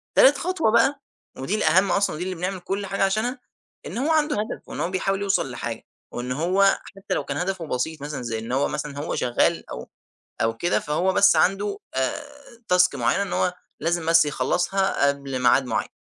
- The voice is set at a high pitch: No, medium, 180 Hz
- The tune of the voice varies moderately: No, wide, 5.9 semitones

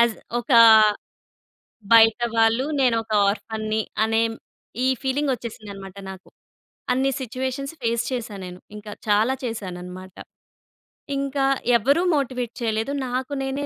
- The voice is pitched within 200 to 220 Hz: No, high, 230 Hz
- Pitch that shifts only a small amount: No, average, 3.3 semitones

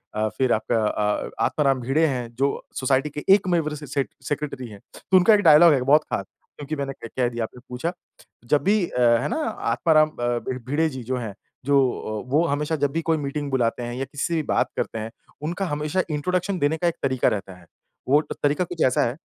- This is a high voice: No, medium, 145 Hz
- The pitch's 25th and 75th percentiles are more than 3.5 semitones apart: Yes, average, 4.1 semitones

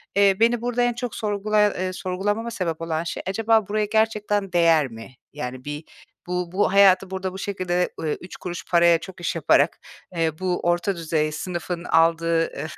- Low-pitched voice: No, medium, 180 Hz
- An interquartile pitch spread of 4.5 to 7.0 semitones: No, average, 3.7 semitones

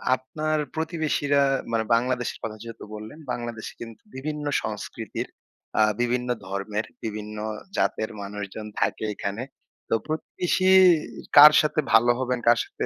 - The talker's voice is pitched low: Yes, low, 120 Hz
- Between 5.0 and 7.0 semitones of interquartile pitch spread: Yes, average, 5.3 semitones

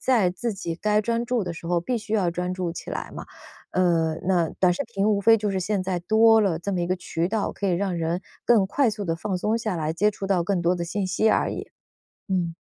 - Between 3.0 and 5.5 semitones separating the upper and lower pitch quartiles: Yes, average, 3.4 semitones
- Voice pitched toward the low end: No, high, 190 Hz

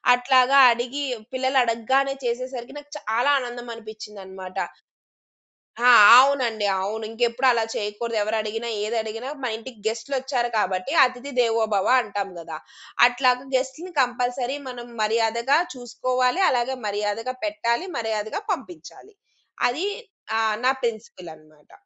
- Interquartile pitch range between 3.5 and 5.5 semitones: No, average, 3.0 semitones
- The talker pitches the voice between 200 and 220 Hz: No, high, 240 Hz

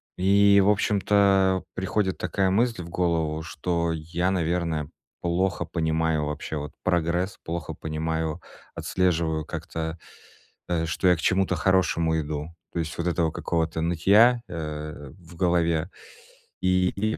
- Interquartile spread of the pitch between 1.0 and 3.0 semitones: Yes, average, 2.7 semitones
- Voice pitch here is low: Yes, very low, 85 Hz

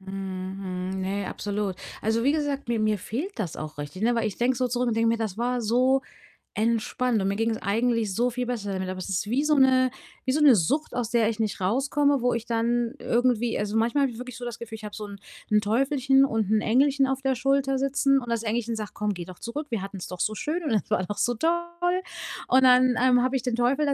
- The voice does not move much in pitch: No, average, 3.8 semitones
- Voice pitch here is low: No, high, 235 Hz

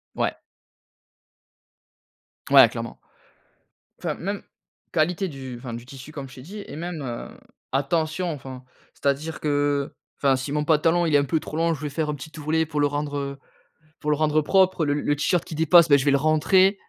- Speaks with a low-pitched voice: No, medium, 150 Hz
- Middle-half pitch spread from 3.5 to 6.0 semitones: No, average, 2.7 semitones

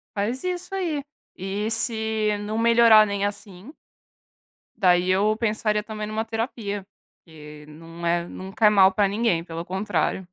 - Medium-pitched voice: No, high, 210 Hz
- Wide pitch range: No, average, 3.1 semitones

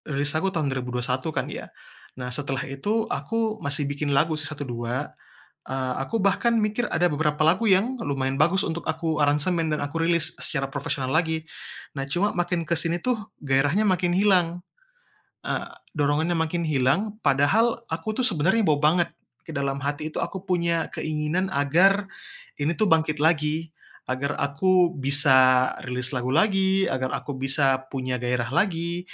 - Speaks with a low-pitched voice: No, medium, 155 Hz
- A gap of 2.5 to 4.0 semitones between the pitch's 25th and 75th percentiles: No, average, 4.5 semitones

